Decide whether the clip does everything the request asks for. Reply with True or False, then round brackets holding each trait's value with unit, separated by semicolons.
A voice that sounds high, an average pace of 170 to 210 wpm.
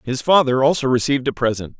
False (130 Hz; 200 wpm)